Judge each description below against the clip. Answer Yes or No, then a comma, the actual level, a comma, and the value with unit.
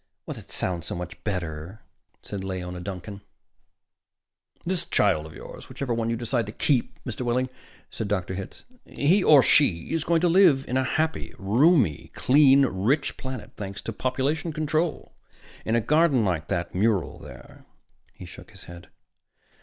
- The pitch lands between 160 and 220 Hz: No, low, 115 Hz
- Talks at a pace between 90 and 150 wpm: No, average, 160 wpm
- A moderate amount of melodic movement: No, wide, 7.3 semitones